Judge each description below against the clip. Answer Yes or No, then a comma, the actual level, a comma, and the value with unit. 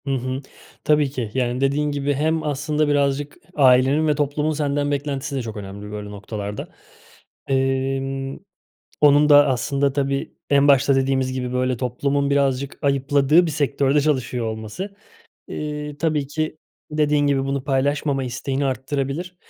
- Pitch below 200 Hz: Yes, medium, 140 Hz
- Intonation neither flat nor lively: No, narrow, 1.8 semitones